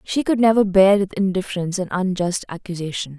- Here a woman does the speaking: Yes, female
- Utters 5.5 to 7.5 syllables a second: Yes, 5.9 syllables/s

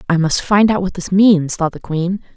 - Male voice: No, female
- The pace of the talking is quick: Yes, fast, 255 wpm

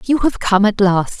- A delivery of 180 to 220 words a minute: No, fast, 250 wpm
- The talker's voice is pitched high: Yes, high, 215 Hz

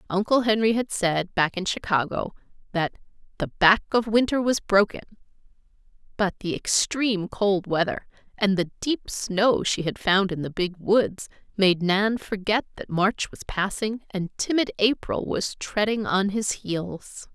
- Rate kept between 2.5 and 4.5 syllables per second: Yes, 4.2 syllables/s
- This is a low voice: No, high, 200 Hz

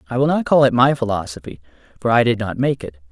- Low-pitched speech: Yes, low, 125 Hz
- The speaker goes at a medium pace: No, fast, 250 wpm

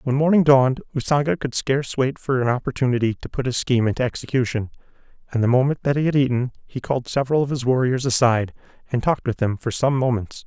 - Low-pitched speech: Yes, low, 130 Hz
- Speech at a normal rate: No, fast, 210 wpm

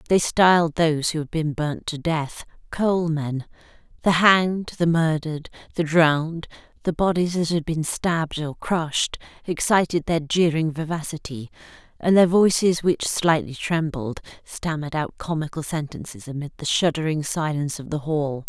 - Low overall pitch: No, medium, 160 Hz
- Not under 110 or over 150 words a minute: Yes, average, 145 wpm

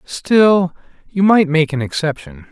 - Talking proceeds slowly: No, average, 145 wpm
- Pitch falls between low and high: Yes, medium, 160 Hz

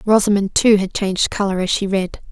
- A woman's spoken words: Yes, female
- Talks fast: Yes, fast, 210 wpm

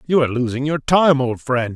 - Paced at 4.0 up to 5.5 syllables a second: Yes, 5.4 syllables/s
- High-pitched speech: No, low, 135 Hz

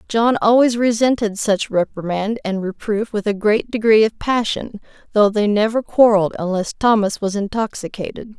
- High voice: Yes, high, 215 Hz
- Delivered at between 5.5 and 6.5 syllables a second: No, 4.9 syllables/s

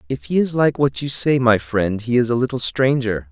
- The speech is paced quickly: Yes, fast, 255 wpm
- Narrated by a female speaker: No, male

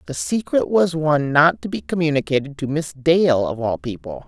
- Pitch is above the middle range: No, medium, 150 Hz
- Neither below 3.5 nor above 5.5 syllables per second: Yes, 5.1 syllables/s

